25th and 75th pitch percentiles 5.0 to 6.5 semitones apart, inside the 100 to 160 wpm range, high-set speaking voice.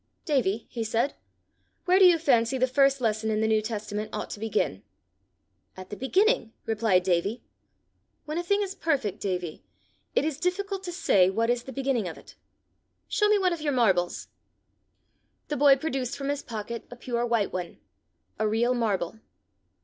No: wide, 5.4 semitones; average, 175 wpm; high, 240 Hz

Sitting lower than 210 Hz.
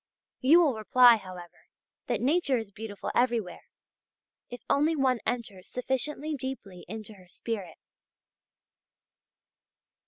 No: high, 235 Hz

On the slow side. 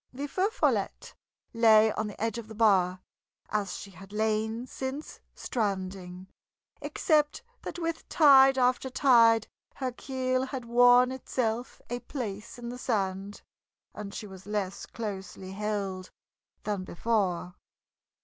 Yes: slow, 130 wpm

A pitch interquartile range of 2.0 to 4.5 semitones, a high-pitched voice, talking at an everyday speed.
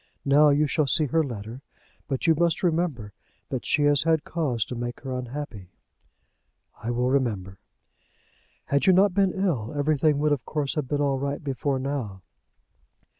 No: average, 3.7 semitones; medium, 140 Hz; average, 170 wpm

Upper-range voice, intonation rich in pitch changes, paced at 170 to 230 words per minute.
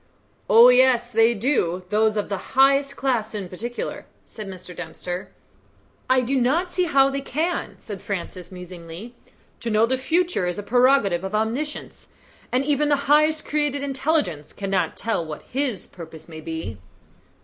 No: high, 230 Hz; wide, 6.9 semitones; average, 160 wpm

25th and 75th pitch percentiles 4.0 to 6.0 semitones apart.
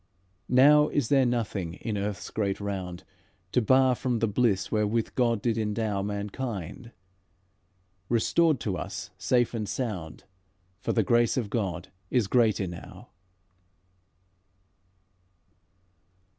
No: average, 3.6 semitones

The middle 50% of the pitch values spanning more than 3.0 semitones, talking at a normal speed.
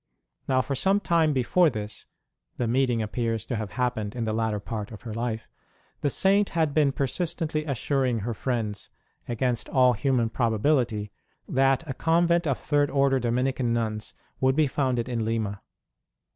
Yes: average, 4.0 semitones; average, 160 wpm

